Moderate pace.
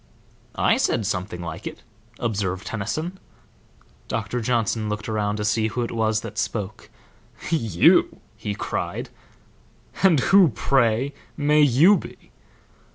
No: slow, 125 wpm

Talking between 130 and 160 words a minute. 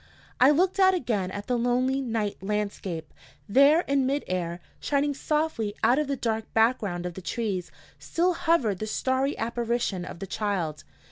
No: average, 175 wpm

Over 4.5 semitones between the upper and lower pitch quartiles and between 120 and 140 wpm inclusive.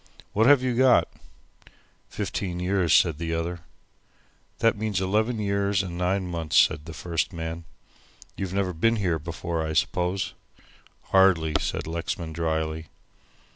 No: average, 3.2 semitones; slow, 135 wpm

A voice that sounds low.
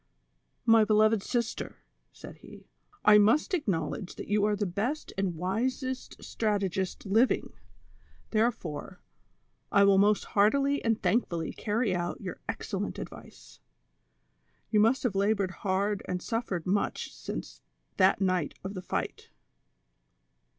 No: high, 205 Hz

